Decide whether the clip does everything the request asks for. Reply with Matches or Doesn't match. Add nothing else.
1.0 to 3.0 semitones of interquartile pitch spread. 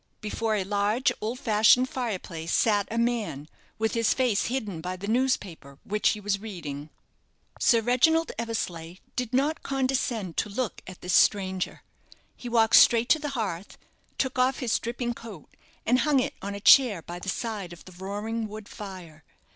Doesn't match